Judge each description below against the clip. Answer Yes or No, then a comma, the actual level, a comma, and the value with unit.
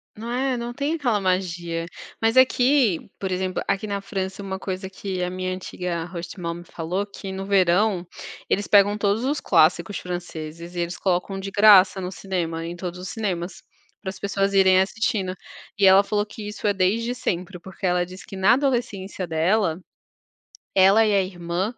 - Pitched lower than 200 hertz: Yes, high, 190 Hz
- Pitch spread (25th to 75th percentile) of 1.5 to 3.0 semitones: Yes, narrow, 2.5 semitones